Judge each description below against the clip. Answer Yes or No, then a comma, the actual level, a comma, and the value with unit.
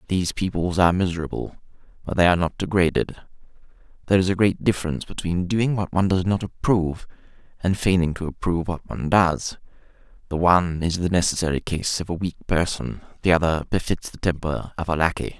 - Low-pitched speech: Yes, very low, 90 Hz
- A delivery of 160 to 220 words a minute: Yes, average, 180 wpm